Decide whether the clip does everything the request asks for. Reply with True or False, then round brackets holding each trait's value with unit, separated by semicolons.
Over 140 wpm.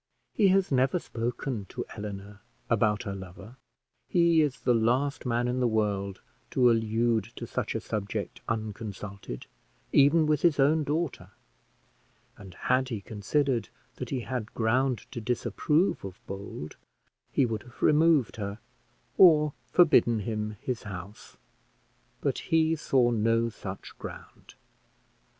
False (135 wpm)